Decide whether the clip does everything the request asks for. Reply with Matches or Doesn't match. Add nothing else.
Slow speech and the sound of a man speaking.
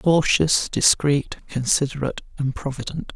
Matches